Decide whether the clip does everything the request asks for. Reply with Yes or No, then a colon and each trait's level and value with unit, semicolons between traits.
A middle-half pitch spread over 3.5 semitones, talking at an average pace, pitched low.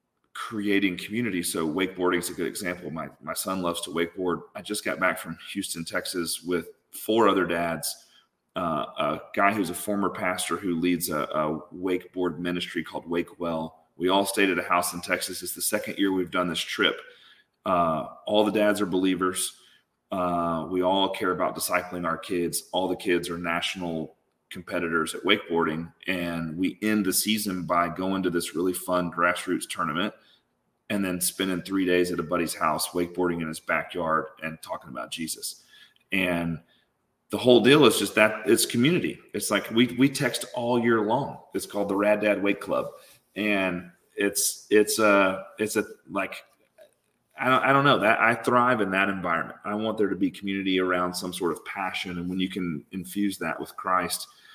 No: average, 2.8 semitones; average, 185 wpm; very low, 90 Hz